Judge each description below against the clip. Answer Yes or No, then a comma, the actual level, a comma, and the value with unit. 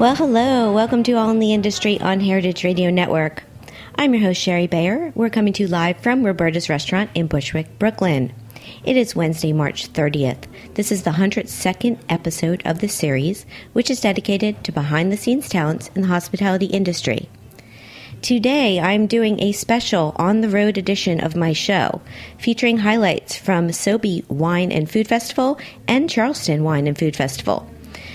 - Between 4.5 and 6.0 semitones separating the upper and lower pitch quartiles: Yes, average, 5.1 semitones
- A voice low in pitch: No, high, 190 Hz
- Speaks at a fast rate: No, average, 170 wpm